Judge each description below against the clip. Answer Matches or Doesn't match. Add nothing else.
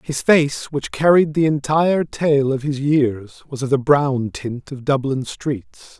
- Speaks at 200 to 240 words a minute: Doesn't match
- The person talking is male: Matches